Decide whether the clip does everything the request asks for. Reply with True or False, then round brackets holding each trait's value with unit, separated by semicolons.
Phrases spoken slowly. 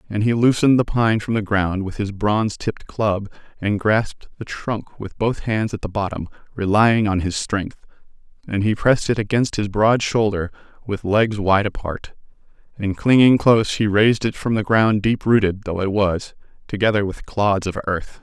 False (190 wpm)